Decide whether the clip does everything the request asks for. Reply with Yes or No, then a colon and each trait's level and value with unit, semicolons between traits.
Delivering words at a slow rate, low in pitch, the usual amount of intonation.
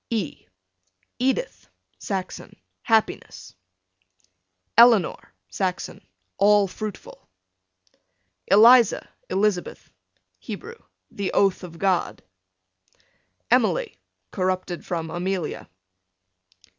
No: slow, 70 wpm; high, 195 Hz; average, 3.2 semitones